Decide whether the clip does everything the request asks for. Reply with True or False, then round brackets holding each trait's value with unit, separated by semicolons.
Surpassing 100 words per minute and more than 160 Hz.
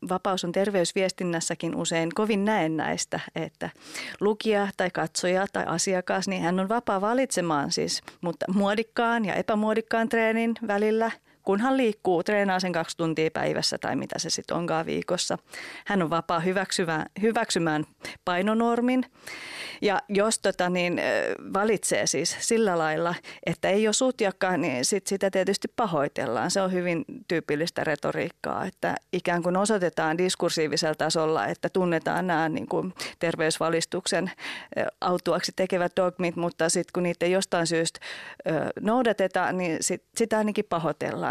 True (135 wpm; 185 Hz)